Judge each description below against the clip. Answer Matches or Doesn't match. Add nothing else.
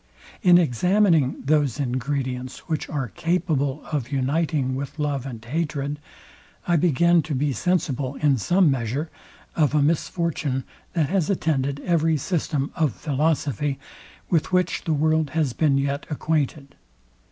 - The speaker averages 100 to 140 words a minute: Matches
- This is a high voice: Doesn't match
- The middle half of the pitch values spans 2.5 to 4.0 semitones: Matches